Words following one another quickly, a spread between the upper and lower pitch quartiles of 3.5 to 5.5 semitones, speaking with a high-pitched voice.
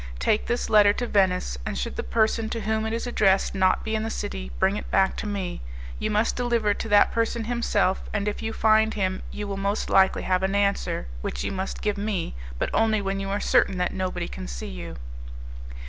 No: fast, 225 wpm; narrow, 2.5 semitones; high, 205 Hz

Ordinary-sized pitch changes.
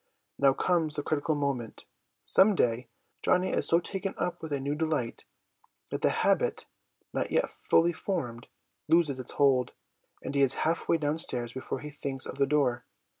Yes: average, 3.8 semitones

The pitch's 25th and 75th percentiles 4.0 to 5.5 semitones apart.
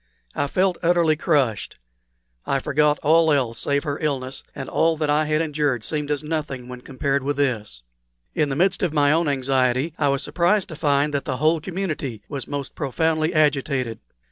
No: narrow, 2.5 semitones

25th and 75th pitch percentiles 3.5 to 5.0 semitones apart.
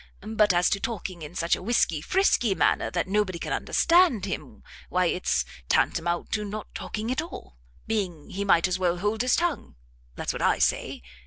Yes: average, 4.0 semitones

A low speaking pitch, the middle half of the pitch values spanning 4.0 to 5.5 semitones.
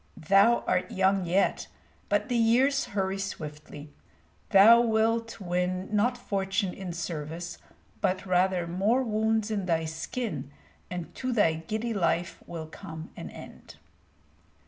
No: high, 190 Hz; average, 4.5 semitones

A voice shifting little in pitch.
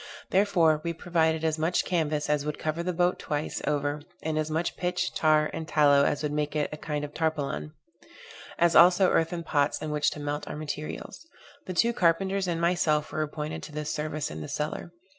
Yes: narrow, 2.2 semitones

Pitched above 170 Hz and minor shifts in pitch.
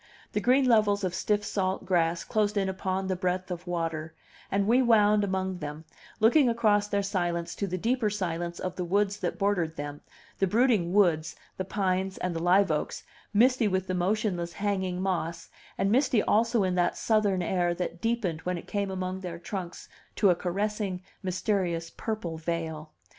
No: high, 190 Hz; average, 3.0 semitones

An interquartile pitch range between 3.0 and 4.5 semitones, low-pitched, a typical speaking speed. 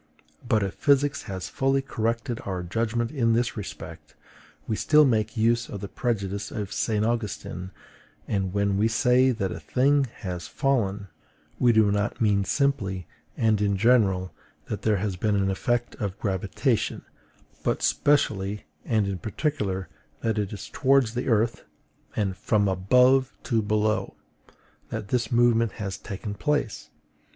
Yes: average, 3.4 semitones; low, 110 Hz; average, 150 wpm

